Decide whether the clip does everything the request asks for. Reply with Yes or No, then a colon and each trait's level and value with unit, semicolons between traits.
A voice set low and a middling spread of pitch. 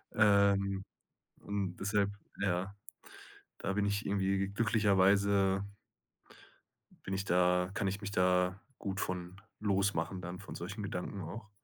No: low, 100 Hz; narrow, 1.5 semitones